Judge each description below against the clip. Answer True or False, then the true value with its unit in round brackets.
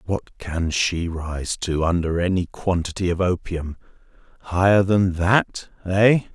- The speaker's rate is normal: False (125 wpm)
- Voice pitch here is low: True (90 Hz)